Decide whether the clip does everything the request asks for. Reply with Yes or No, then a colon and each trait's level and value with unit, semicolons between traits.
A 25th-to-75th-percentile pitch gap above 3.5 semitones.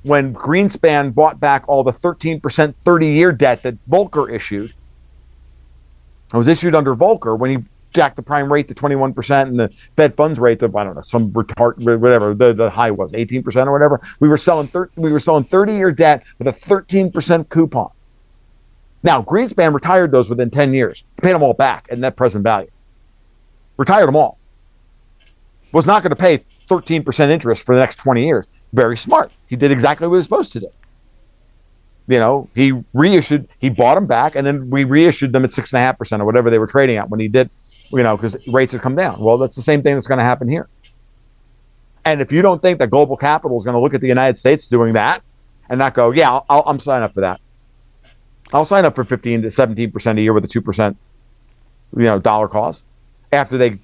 Yes: average, 4.3 semitones